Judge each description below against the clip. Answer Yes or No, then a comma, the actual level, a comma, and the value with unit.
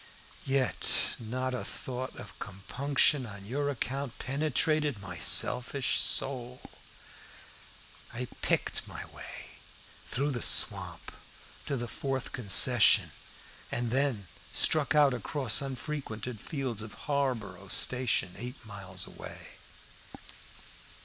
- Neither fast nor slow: No, slow, 105 wpm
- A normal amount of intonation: Yes, average, 4.0 semitones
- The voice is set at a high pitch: No, low, 125 Hz